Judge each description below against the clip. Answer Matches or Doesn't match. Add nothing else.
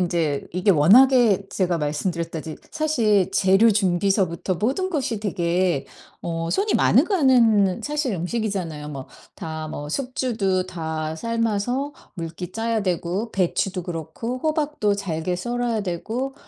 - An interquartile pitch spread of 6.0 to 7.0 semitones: Doesn't match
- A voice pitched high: Matches